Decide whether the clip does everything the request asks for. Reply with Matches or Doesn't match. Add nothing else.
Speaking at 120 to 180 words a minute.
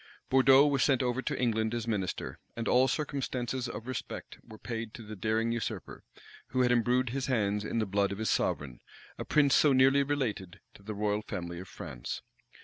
Doesn't match